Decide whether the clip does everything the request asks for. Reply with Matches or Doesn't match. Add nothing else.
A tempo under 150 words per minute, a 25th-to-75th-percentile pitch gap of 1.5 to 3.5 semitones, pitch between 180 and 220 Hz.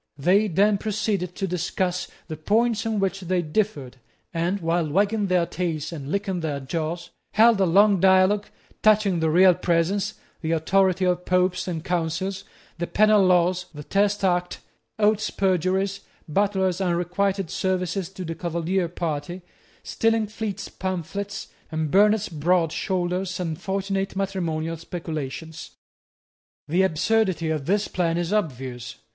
Matches